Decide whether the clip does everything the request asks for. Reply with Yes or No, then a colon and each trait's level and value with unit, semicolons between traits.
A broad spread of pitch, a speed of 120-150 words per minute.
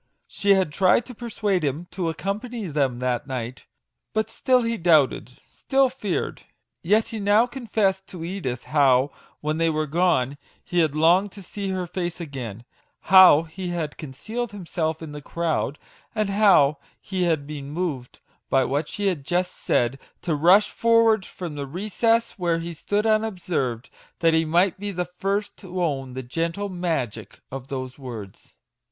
No: wide, 5.7 semitones; average, 170 wpm